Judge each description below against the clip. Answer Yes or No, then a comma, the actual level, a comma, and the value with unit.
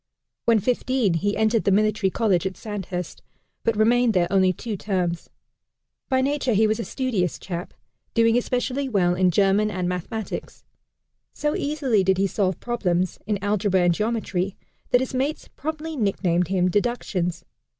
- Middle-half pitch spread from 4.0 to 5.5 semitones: Yes, average, 4.5 semitones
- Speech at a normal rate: Yes, average, 155 wpm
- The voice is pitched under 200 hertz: No, high, 210 Hz